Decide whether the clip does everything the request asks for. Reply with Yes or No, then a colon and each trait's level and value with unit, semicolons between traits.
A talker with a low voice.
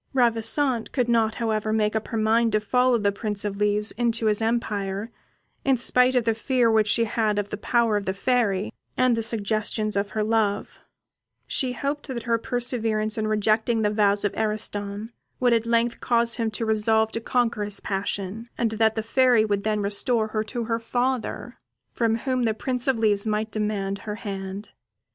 No: high, 220 Hz